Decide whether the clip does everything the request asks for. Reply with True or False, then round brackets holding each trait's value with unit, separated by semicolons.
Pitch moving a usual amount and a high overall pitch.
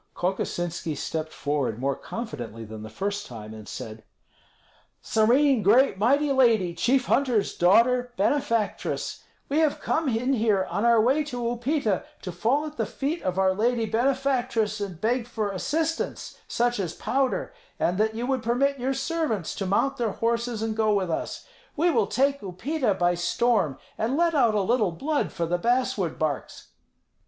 False (6.0 semitones; 225 Hz)